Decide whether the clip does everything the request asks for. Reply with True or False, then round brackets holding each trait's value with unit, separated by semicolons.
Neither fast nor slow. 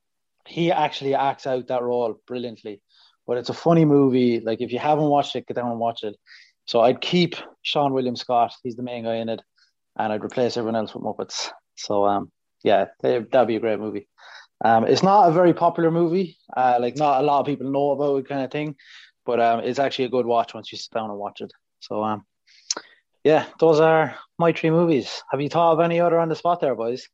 False (230 wpm)